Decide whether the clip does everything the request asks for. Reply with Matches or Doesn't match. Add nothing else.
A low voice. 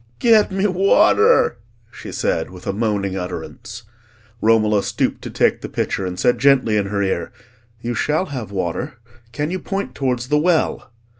Matches